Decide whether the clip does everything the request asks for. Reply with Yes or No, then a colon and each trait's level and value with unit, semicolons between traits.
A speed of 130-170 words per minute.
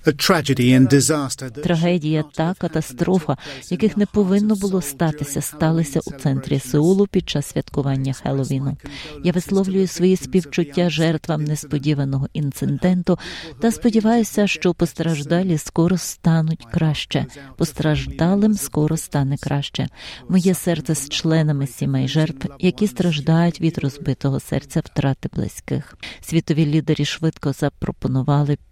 No: slow, 105 wpm